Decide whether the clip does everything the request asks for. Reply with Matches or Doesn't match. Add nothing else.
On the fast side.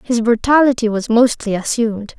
Doesn't match